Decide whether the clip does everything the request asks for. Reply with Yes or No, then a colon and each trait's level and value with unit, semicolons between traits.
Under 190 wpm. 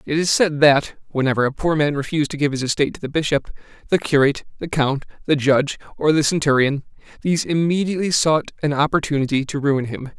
No: average, 195 wpm